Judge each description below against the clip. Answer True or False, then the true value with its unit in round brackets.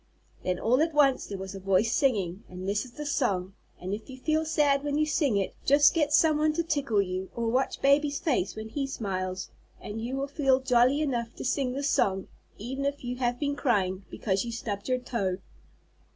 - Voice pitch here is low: False (250 Hz)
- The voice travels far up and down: True (6.0 semitones)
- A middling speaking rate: False (215 wpm)